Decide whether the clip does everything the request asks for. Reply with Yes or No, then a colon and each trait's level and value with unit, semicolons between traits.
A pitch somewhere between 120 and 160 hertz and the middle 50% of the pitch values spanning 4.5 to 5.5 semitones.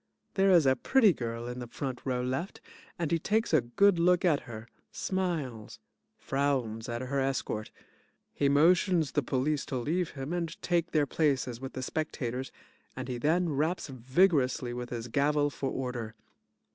Yes: medium, 140 Hz; average, 5.1 semitones